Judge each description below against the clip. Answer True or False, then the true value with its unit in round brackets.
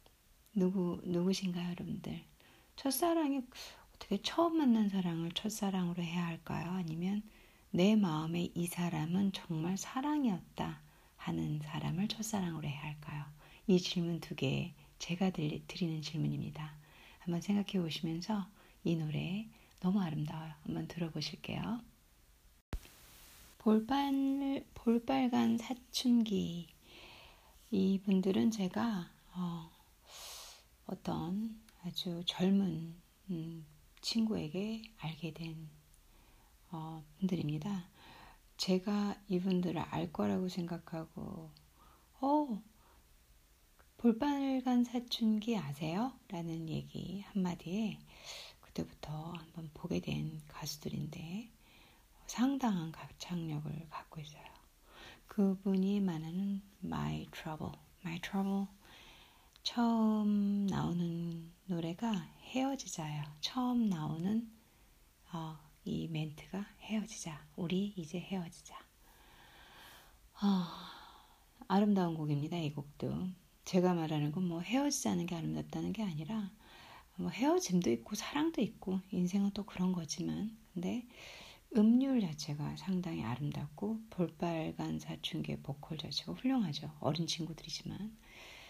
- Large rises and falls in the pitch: False (4.5 semitones)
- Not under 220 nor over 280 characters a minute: True (240 characters per minute)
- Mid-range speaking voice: True (180 Hz)